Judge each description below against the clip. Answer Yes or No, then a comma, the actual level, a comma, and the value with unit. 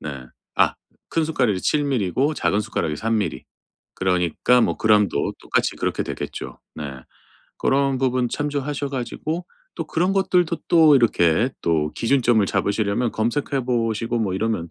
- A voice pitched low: Yes, low, 120 Hz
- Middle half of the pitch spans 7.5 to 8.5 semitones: No, wide, 5.7 semitones